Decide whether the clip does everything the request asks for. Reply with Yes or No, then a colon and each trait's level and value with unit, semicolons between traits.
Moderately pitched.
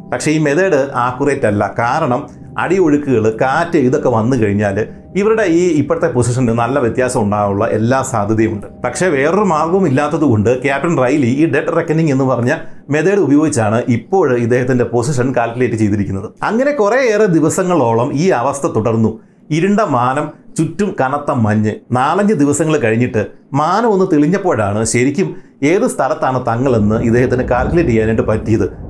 No: low, 125 Hz